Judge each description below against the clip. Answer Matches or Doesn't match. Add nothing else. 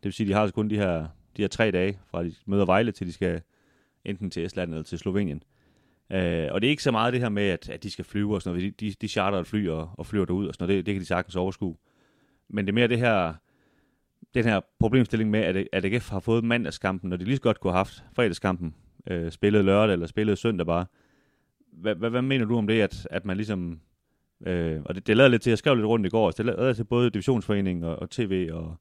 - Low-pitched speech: Matches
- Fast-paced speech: Matches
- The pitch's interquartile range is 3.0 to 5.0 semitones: Matches